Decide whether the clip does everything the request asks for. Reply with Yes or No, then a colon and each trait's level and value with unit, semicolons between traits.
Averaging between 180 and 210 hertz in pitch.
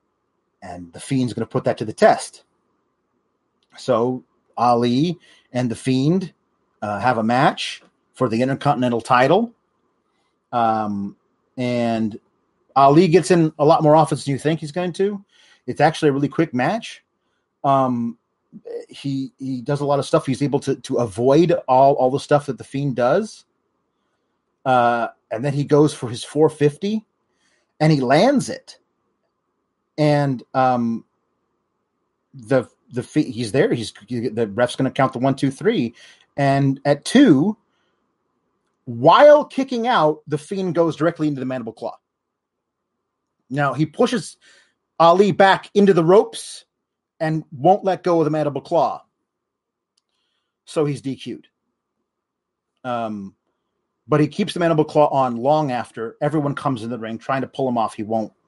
No: medium, 140 Hz